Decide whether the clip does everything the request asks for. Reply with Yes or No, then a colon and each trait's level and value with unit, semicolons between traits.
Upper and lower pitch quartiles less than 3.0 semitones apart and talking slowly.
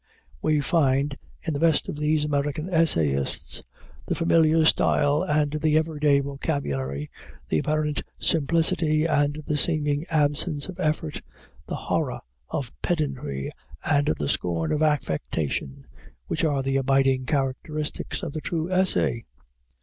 Yes: narrow, 2.5 semitones; slow, 130 wpm